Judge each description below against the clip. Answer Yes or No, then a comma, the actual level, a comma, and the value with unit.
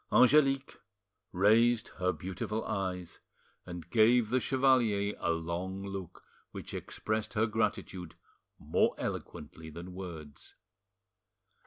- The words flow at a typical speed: No, slow, 105 wpm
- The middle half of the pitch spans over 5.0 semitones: No, average, 4.2 semitones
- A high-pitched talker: No, low, 100 Hz